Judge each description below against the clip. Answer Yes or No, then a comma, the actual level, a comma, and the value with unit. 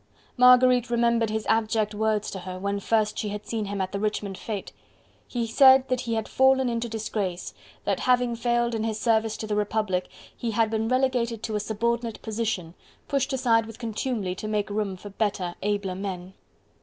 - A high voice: Yes, high, 220 Hz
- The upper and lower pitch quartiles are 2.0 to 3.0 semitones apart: Yes, narrow, 2.4 semitones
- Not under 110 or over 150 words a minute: No, average, 190 wpm